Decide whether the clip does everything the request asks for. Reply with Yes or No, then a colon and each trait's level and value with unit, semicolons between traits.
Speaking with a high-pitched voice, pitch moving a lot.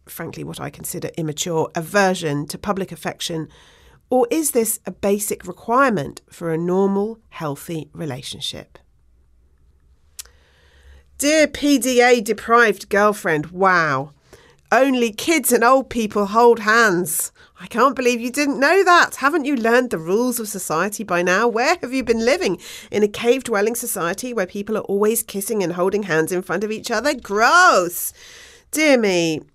Yes: high, 205 Hz; wide, 6.2 semitones